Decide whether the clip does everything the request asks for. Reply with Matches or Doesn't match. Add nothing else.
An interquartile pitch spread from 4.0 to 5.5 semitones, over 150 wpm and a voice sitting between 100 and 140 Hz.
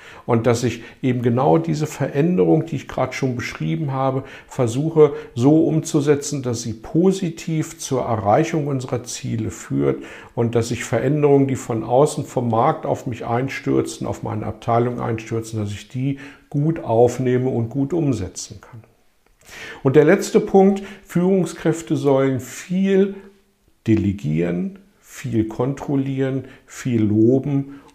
Doesn't match